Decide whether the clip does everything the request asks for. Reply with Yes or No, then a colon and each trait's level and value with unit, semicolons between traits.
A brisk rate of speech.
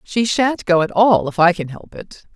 Yes: fast, 255 wpm